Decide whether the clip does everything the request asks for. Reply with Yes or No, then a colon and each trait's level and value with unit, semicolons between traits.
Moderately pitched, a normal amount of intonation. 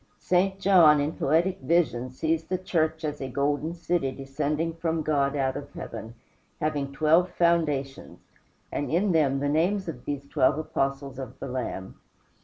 Yes: medium, 150 Hz; average, 3.4 semitones